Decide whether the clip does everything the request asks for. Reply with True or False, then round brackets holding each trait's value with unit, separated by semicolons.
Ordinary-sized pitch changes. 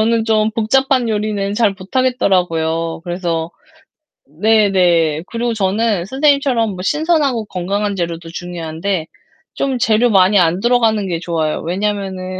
True (4.6 semitones)